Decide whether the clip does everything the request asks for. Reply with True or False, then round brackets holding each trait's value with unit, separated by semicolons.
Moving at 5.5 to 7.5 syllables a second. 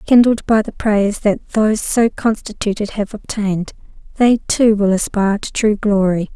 False (4.9 syllables/s)